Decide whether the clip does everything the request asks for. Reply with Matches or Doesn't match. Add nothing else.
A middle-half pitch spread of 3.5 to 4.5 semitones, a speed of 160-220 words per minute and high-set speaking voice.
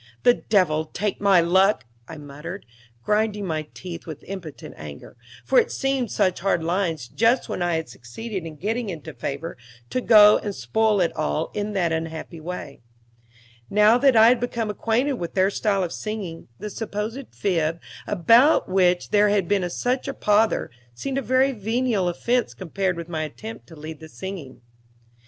Doesn't match